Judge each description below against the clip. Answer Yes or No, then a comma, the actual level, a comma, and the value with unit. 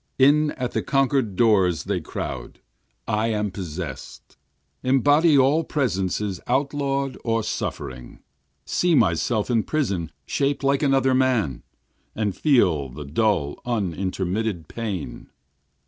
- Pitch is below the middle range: Yes, low, 110 Hz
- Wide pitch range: Yes, wide, 6.8 semitones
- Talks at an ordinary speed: No, slow, 115 wpm